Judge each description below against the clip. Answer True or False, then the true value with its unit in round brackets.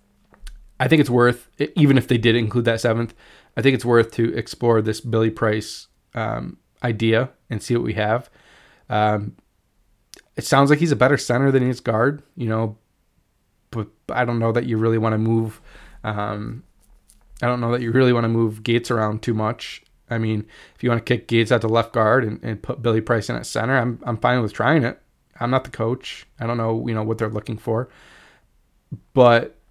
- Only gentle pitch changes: True (1.9 semitones)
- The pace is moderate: False (210 wpm)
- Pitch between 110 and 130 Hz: True (115 Hz)